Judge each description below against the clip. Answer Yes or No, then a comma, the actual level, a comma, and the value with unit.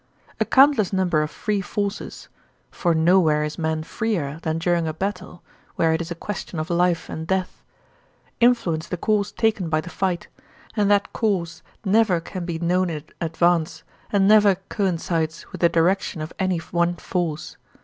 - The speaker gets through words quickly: No, average, 170 wpm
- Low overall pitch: No, medium, 175 Hz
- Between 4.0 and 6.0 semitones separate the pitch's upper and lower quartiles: No, average, 3.2 semitones